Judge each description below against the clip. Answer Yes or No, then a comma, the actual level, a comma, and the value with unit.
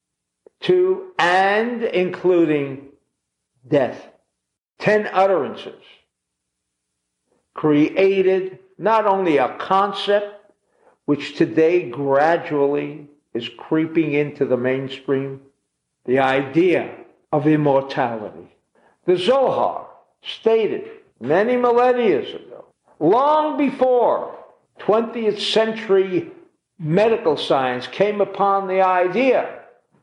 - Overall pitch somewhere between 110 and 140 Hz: No, high, 190 Hz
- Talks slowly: Yes, slow, 80 wpm